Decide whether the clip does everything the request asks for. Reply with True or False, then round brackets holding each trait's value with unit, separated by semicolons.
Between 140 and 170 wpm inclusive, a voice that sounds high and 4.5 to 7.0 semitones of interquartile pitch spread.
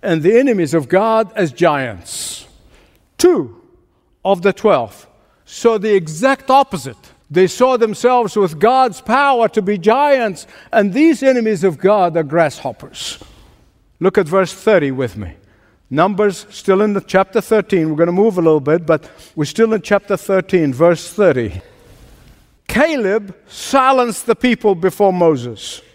True (150 wpm; 195 Hz; 5.3 semitones)